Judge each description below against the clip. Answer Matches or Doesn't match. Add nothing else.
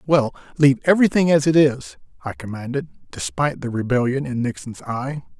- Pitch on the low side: Matches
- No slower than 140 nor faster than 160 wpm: Matches